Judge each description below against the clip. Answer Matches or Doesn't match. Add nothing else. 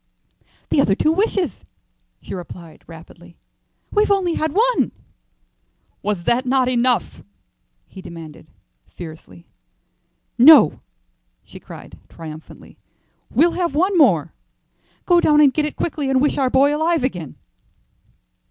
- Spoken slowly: Matches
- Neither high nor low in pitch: Doesn't match